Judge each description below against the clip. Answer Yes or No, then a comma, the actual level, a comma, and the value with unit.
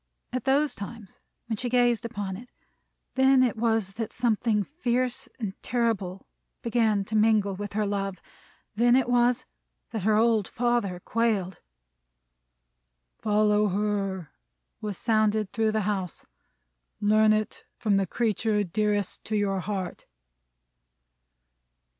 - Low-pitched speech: No, high, 215 Hz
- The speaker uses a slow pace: Yes, slow, 125 wpm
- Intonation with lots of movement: No, average, 2.7 semitones